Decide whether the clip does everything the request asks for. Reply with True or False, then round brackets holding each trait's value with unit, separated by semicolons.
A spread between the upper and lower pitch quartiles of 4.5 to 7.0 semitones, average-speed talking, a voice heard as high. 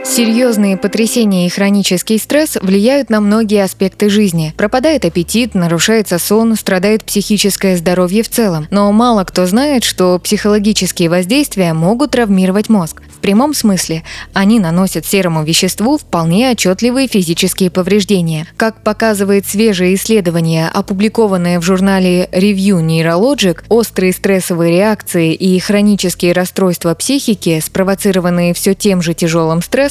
False (3.3 semitones; 125 wpm; 195 Hz)